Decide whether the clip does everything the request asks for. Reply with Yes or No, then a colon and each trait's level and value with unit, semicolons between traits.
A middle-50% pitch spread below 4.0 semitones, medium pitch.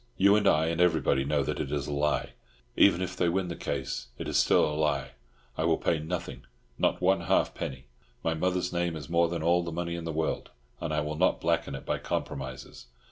No: average, 2.7 semitones; very low, 80 Hz